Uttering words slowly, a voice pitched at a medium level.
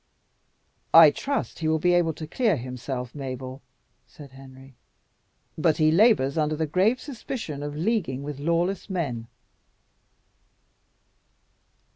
Yes: slow, 120 wpm; medium, 155 Hz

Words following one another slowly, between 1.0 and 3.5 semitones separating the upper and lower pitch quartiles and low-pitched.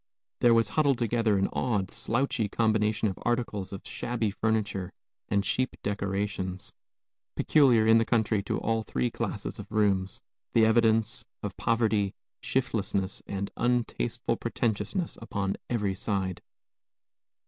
Yes: slow, 125 wpm; average, 2.9 semitones; low, 110 Hz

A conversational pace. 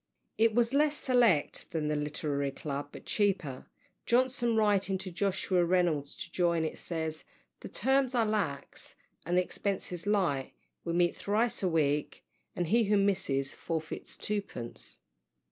Yes: average, 150 wpm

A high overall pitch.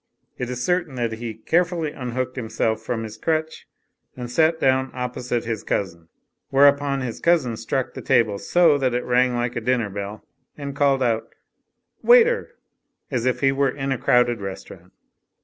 No: low, 125 Hz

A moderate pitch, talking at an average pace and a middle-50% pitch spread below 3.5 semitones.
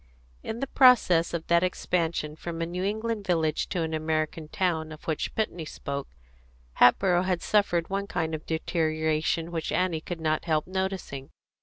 Yes: medium, 165 Hz; average, 165 wpm; average, 2.7 semitones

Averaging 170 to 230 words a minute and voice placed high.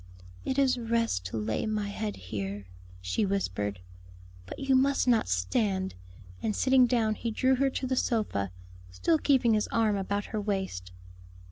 No: average, 160 wpm; high, 215 Hz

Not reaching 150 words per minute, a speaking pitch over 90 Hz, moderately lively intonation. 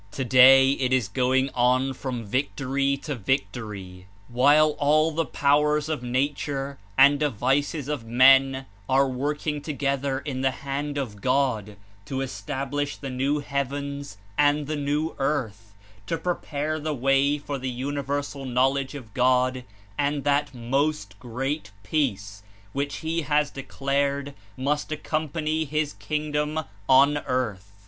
No: slow, 135 wpm; medium, 140 Hz; narrow, 2.2 semitones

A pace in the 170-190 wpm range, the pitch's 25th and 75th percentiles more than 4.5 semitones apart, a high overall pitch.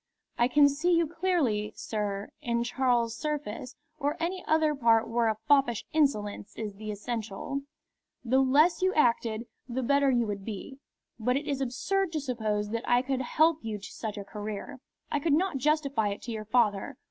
Yes: average, 180 wpm; average, 5.0 semitones; high, 245 Hz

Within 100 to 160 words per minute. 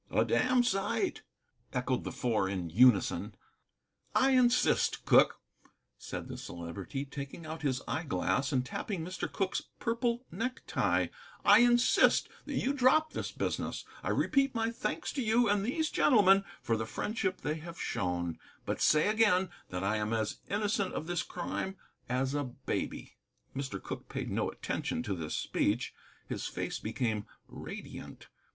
Yes: average, 150 wpm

